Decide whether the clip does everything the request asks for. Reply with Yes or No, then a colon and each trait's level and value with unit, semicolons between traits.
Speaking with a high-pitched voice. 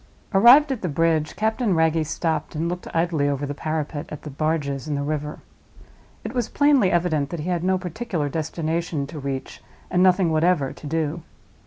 No: medium, 160 Hz